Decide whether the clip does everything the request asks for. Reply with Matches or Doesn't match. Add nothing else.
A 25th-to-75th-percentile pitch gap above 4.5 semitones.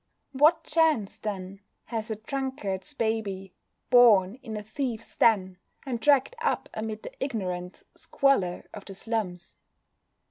Matches